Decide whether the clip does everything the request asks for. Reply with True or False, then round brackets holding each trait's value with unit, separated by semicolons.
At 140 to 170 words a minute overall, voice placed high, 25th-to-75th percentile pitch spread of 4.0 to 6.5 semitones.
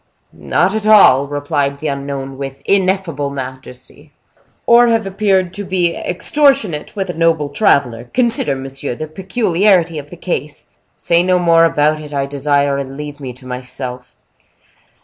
False (150 wpm; 150 Hz; 5.2 semitones)